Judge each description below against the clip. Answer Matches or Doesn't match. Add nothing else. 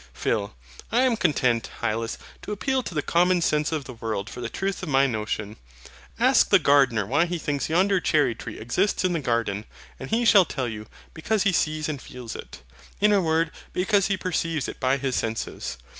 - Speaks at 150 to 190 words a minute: Doesn't match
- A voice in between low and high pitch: Matches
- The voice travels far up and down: Matches